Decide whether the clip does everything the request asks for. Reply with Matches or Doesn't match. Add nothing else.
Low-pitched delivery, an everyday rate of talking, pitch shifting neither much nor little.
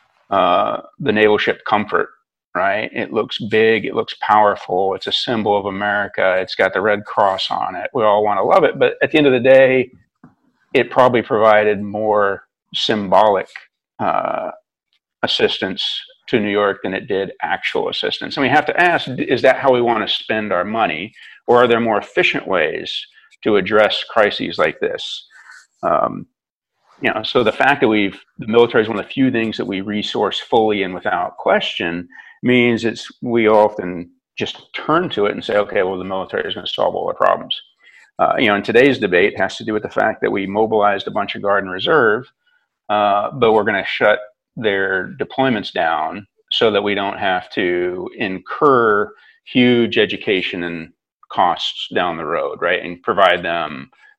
Matches